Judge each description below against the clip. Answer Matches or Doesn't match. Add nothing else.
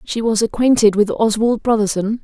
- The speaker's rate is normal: Matches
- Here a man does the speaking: Doesn't match